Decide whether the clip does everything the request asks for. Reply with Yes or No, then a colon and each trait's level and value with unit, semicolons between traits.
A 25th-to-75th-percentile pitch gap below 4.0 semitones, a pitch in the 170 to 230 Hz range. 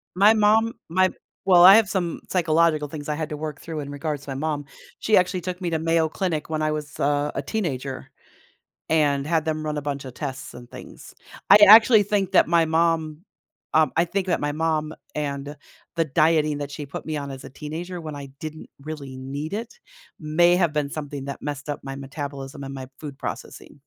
No: average, 2.9 semitones; medium, 155 Hz